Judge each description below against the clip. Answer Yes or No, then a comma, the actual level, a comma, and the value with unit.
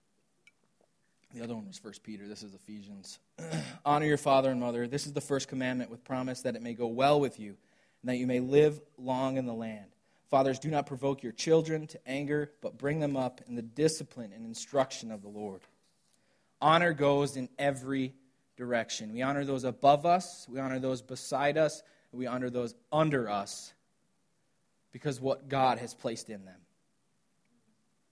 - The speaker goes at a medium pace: Yes, average, 180 wpm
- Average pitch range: Yes, average, 3.4 semitones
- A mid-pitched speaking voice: No, low, 130 Hz